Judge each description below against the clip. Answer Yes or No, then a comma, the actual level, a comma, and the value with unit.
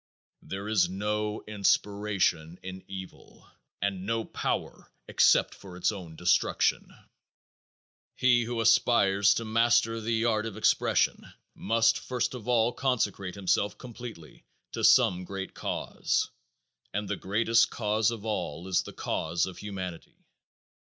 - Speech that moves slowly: Yes, slow, 130 wpm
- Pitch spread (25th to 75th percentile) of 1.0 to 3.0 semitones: No, average, 3.4 semitones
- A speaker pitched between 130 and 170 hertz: No, low, 105 Hz